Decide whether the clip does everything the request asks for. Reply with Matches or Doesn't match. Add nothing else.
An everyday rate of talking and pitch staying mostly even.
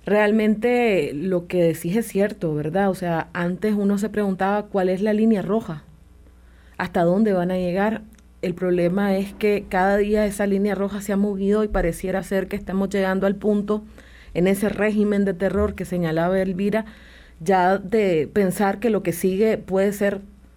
Matches